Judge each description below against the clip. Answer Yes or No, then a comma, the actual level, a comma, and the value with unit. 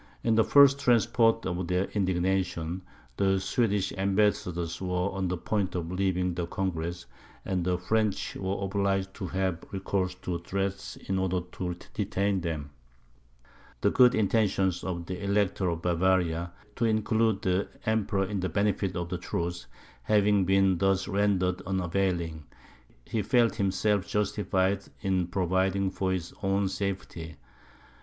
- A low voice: Yes, very low, 95 Hz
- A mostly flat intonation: Yes, narrow, 1.9 semitones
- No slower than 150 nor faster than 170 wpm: No, average, 140 wpm